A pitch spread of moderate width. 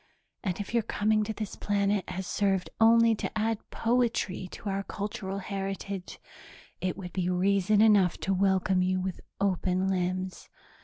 No: narrow, 2.2 semitones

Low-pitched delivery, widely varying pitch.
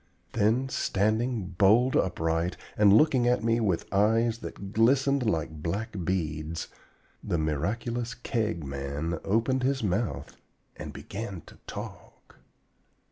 Yes: low, 105 Hz; wide, 6.0 semitones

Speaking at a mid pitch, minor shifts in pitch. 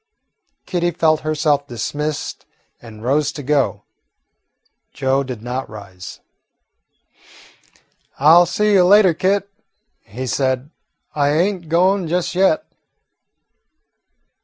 No: medium, 150 Hz; average, 5.2 semitones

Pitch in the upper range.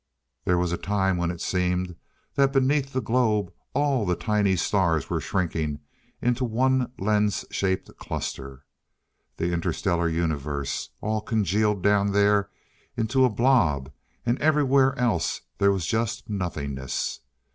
No: low, 100 Hz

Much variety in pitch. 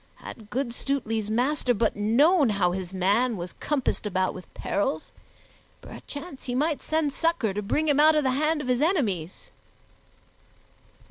Yes: wide, 6.4 semitones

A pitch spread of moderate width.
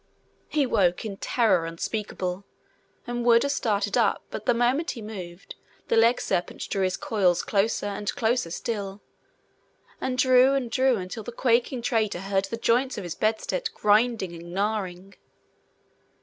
Yes: average, 3.9 semitones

